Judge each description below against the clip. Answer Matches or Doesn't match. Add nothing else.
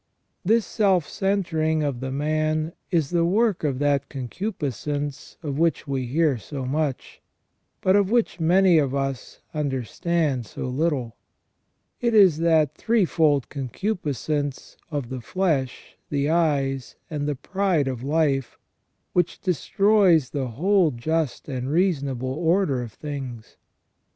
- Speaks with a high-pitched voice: Doesn't match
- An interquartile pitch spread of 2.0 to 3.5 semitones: Doesn't match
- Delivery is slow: Matches